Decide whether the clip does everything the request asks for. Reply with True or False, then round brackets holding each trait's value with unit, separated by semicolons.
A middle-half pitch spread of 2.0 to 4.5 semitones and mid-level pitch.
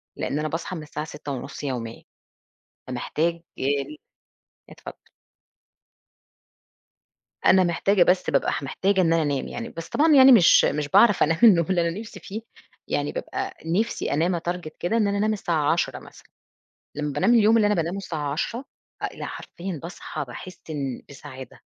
False (5.2 semitones; 170 Hz)